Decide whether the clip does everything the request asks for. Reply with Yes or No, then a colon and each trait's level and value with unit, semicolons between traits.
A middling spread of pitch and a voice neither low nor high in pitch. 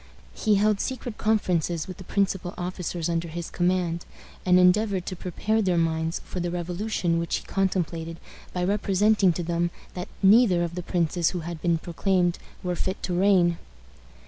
No: narrow, 2.2 semitones; medium, 180 Hz